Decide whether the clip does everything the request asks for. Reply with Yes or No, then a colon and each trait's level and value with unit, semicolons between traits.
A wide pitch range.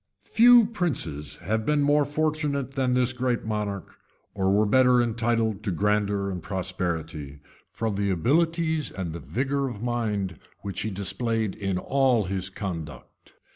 Yes: wide, 5.7 semitones